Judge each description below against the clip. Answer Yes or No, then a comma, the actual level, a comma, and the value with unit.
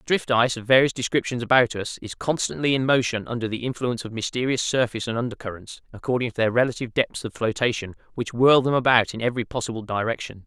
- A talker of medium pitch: No, low, 120 Hz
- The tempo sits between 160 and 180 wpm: No, fast, 205 wpm